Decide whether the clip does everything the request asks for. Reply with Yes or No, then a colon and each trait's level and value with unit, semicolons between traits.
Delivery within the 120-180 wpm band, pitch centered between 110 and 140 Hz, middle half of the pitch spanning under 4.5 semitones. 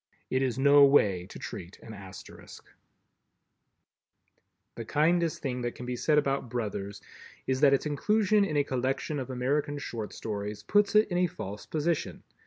No: average, 165 wpm; low, 135 Hz; average, 4.9 semitones